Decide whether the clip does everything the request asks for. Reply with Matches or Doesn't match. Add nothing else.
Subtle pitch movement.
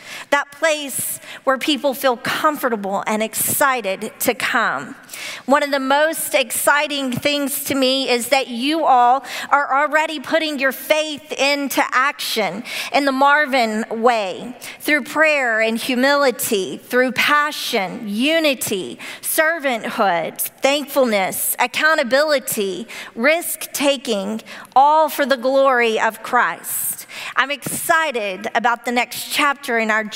Doesn't match